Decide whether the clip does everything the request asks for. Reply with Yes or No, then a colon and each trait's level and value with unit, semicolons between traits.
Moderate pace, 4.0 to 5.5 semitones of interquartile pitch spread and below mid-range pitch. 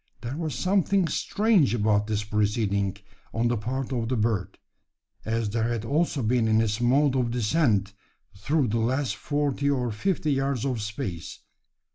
Yes: average, 160 wpm; average, 4.6 semitones; low, 120 Hz